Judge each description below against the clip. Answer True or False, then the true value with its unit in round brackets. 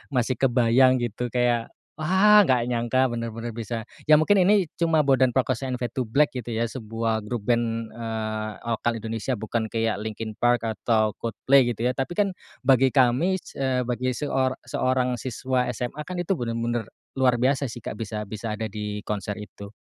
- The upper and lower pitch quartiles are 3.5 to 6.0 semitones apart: False (2.7 semitones)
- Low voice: True (120 Hz)